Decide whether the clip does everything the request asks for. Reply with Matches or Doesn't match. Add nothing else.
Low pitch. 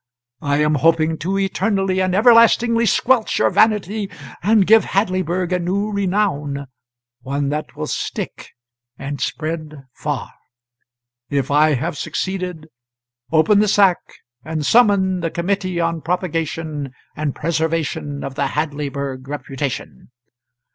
Doesn't match